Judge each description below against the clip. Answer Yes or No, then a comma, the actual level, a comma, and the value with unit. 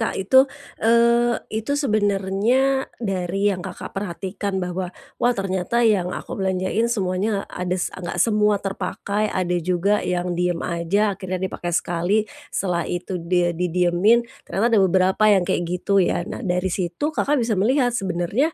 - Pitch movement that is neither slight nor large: Yes, average, 3.3 semitones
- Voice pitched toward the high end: Yes, high, 195 Hz